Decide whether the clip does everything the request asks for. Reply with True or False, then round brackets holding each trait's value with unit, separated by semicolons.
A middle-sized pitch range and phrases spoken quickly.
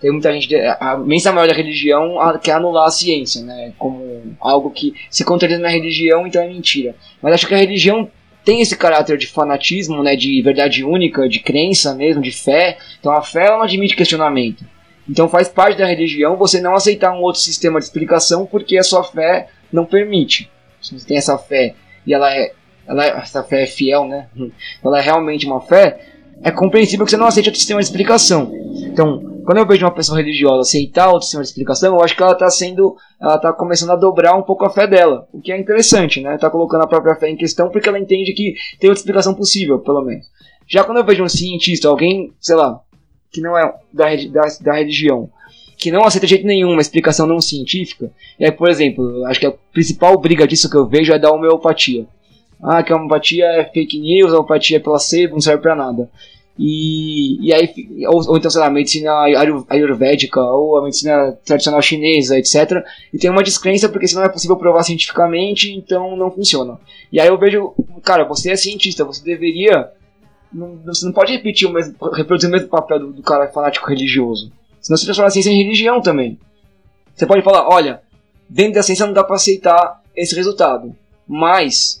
True (4.4 semitones; 205 wpm)